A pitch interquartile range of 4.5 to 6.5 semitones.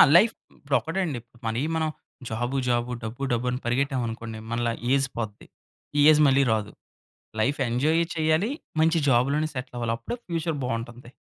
Yes: average, 4.8 semitones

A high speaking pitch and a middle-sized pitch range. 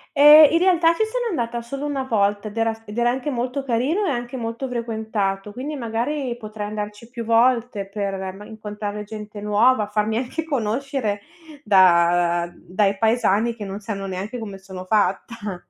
Yes: high, 225 Hz; average, 3.4 semitones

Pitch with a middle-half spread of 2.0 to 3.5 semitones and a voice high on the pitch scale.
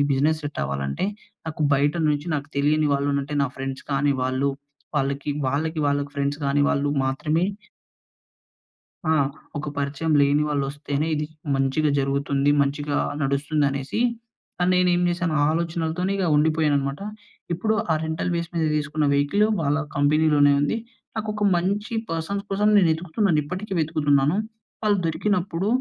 No: average, 3.1 semitones; medium, 150 Hz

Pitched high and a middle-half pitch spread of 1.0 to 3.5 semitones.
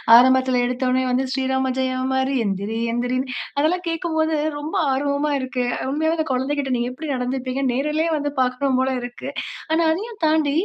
Yes: very high, 265 Hz; average, 2.9 semitones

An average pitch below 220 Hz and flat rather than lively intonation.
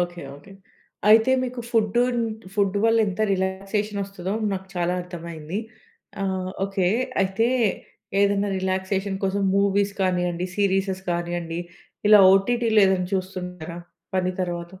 Yes: high, 190 Hz; narrow, 2.0 semitones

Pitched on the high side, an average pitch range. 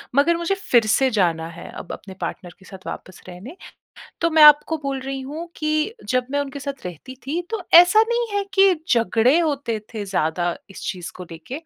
No: very high, 270 Hz; wide, 8.8 semitones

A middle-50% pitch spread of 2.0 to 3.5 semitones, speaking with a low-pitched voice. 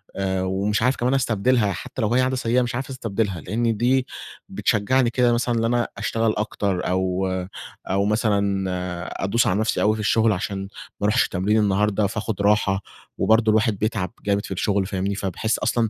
Yes: average, 2.9 semitones; low, 105 Hz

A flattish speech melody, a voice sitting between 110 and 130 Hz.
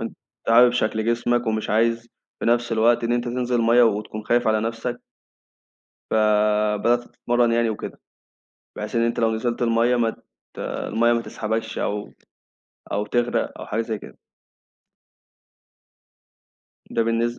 Yes: narrow, 1.5 semitones; low, 115 Hz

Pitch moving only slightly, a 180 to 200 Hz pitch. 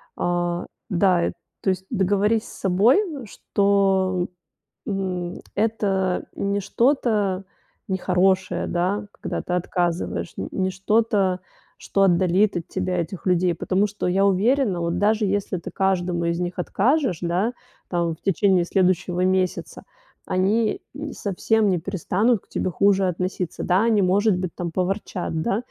Yes: narrow, 2.2 semitones; high, 190 Hz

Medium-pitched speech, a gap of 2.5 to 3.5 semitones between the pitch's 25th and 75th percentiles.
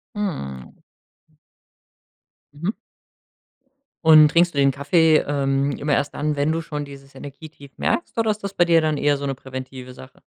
Yes: medium, 145 Hz; average, 2.9 semitones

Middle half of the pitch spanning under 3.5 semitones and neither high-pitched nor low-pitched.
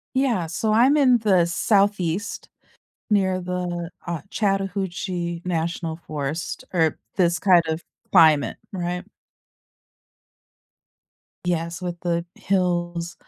Yes: narrow, 2.5 semitones; medium, 175 Hz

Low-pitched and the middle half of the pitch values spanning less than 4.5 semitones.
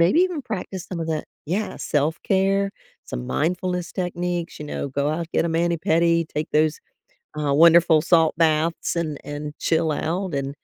No: medium, 165 Hz; narrow, 2.6 semitones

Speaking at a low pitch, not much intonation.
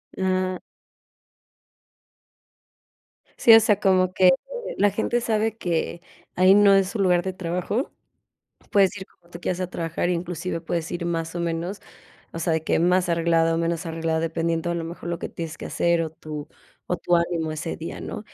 No: medium, 175 Hz; narrow, 2.2 semitones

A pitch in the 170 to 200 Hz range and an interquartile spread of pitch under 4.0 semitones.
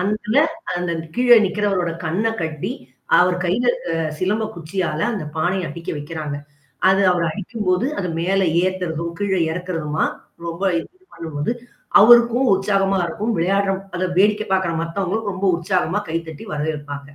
Yes: medium, 185 Hz; average, 3.5 semitones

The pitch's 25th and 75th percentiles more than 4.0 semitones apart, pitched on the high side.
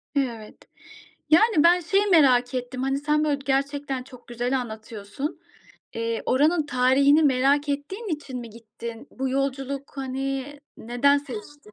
No: average, 2.8 semitones; very high, 270 Hz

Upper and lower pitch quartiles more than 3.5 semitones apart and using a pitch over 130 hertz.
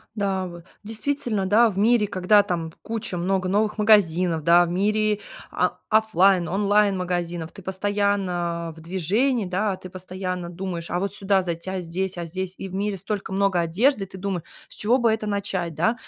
No: average, 2.9 semitones; high, 190 Hz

